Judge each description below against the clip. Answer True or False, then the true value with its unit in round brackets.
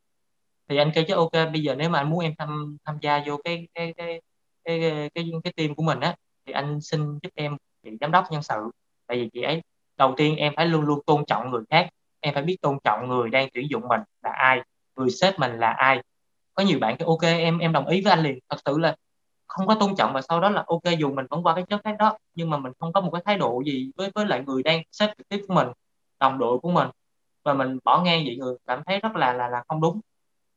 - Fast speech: True (270 wpm)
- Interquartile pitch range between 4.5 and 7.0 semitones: False (4.1 semitones)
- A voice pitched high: False (155 Hz)